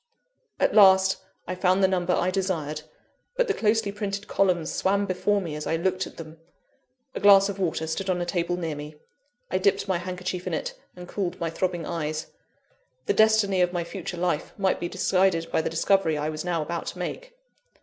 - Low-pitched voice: No, medium, 180 Hz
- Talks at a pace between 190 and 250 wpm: Yes, average, 200 wpm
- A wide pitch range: No, average, 2.7 semitones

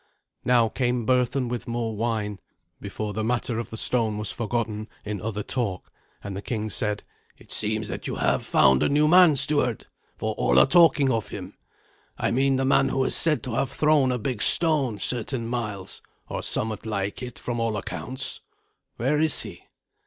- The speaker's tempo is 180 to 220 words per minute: Yes, average, 185 wpm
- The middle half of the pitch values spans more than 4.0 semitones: No, average, 3.6 semitones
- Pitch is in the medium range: No, low, 115 Hz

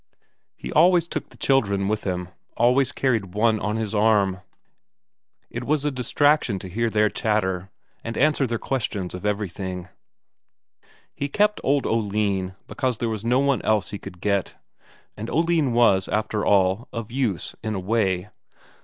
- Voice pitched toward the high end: No, low, 110 Hz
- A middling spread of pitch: Yes, average, 4.6 semitones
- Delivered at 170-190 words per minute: No, average, 160 wpm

